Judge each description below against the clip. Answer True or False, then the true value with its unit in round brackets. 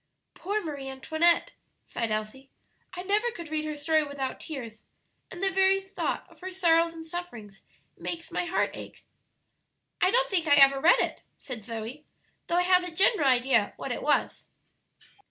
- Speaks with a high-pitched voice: True (320 Hz)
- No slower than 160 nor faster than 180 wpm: True (175 wpm)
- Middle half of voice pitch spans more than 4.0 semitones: True (5.1 semitones)